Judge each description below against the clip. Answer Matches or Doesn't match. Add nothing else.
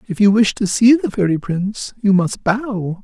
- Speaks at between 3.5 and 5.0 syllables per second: Matches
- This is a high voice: Matches